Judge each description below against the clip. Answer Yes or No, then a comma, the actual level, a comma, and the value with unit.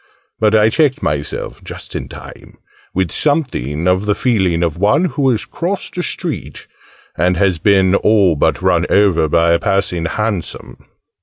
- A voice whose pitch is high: No, very low, 95 Hz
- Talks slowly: No, average, 160 wpm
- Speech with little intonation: No, average, 4.7 semitones